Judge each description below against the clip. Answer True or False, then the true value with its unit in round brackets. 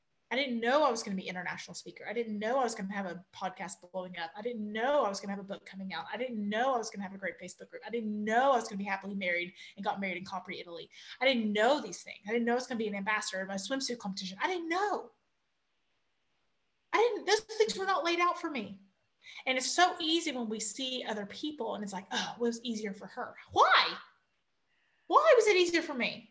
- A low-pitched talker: False (225 Hz)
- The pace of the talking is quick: True (275 wpm)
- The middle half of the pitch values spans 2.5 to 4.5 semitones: False (5.3 semitones)